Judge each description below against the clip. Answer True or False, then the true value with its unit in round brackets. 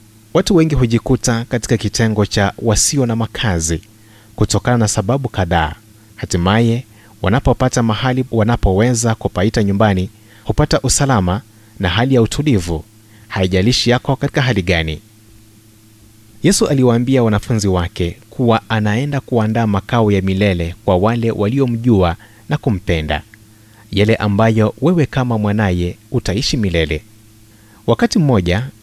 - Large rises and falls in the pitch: False (3.1 semitones)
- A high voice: False (110 Hz)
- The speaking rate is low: False (110 wpm)